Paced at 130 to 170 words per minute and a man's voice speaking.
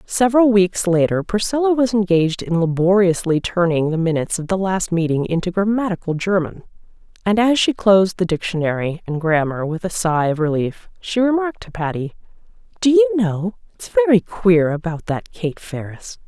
No: average, 165 wpm; female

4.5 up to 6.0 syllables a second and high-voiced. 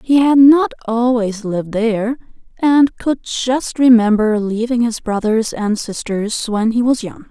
No: 4.1 syllables/s; high, 230 Hz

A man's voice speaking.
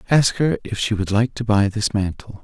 Yes: male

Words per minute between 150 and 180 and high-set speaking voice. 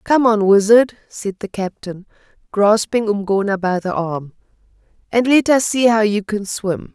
Yes: average, 165 wpm; high, 210 Hz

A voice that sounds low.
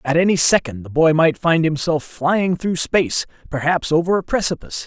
No: medium, 160 Hz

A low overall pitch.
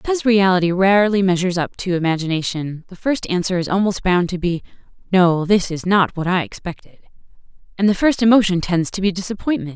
No: medium, 185 Hz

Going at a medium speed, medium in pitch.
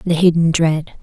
Yes: average, 175 wpm; medium, 165 Hz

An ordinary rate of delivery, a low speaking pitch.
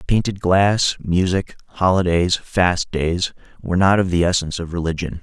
Yes: average, 150 wpm; very low, 90 Hz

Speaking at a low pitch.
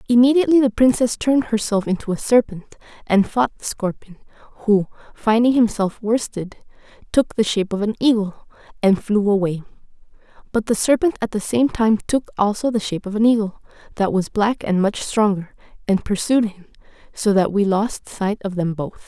No: high, 215 Hz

